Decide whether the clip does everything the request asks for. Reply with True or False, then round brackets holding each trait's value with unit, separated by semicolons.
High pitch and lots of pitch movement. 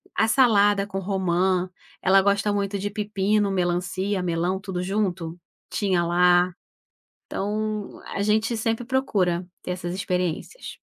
False (195 Hz; 2.5 semitones)